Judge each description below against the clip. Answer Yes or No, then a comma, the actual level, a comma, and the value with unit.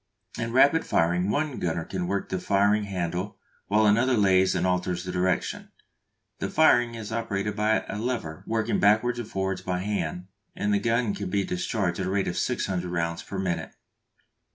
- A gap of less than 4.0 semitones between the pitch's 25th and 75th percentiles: Yes, average, 3.3 semitones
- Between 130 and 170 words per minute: No, average, 180 wpm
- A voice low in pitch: Yes, low, 100 Hz